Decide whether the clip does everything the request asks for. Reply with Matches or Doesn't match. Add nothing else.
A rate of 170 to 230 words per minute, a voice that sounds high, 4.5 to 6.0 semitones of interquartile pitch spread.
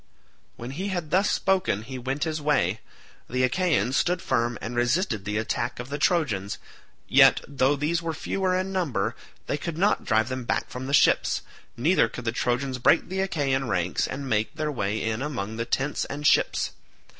Doesn't match